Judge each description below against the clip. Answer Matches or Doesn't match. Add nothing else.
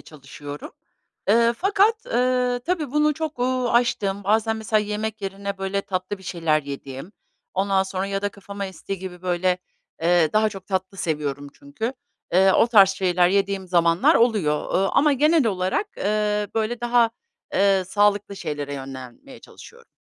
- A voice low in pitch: Doesn't match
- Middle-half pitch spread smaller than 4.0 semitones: Doesn't match